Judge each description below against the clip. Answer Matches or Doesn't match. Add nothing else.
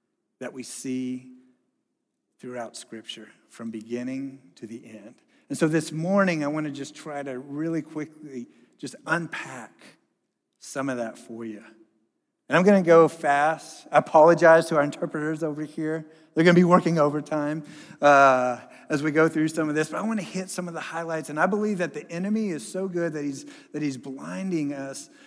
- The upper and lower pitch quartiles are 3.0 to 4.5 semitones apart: Matches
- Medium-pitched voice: Matches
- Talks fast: Doesn't match